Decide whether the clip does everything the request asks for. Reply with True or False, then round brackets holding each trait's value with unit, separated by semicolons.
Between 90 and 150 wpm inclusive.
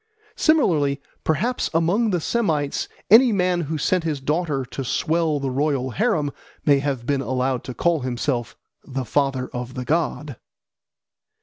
True (145 wpm)